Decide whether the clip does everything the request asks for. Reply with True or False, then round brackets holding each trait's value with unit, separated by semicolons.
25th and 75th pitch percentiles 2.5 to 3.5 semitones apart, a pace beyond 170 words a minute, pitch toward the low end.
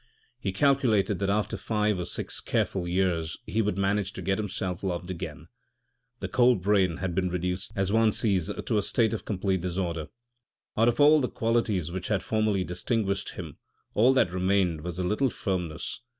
True (3.0 semitones; 180 wpm; 95 Hz)